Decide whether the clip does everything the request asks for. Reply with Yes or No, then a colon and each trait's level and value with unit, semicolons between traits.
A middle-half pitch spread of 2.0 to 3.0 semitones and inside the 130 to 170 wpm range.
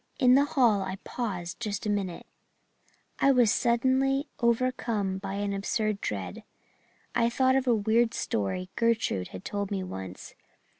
No: average, 4.5 semitones; average, 150 wpm